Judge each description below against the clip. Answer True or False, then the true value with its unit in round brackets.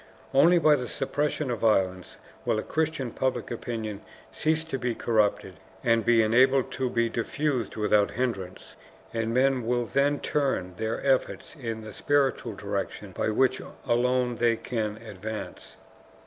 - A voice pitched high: False (120 Hz)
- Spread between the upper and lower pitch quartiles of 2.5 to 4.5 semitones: True (3.5 semitones)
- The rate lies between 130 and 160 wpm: True (150 wpm)